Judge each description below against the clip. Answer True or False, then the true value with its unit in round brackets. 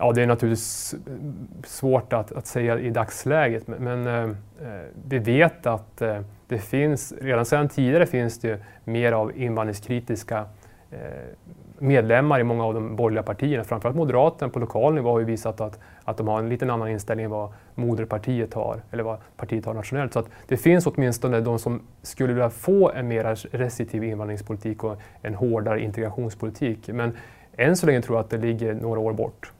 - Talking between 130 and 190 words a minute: True (175 wpm)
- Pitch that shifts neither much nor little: False (2.2 semitones)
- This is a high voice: False (115 Hz)